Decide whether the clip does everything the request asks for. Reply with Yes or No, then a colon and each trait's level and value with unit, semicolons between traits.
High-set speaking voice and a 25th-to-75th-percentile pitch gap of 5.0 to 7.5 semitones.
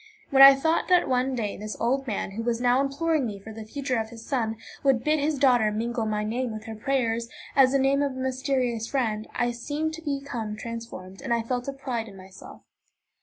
No: high, 245 Hz; average, 3.5 semitones